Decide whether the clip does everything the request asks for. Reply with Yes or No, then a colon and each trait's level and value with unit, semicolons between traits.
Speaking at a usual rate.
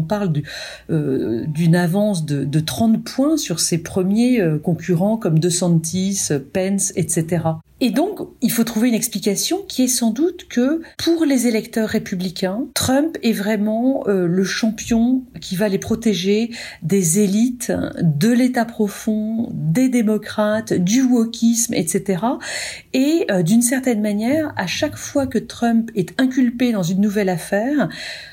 No: slow, 140 wpm